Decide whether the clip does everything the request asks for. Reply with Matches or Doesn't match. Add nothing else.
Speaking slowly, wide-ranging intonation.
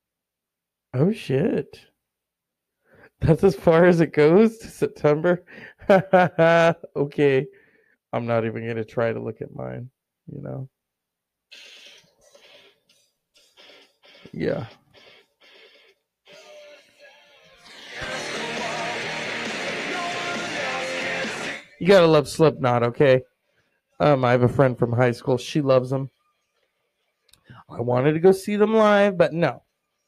Matches